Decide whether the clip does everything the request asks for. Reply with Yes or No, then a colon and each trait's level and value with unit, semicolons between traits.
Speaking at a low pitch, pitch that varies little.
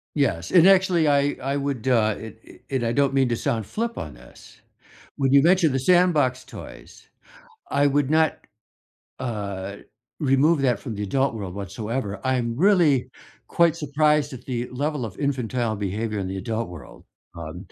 No: low, 130 Hz; average, 5.1 semitones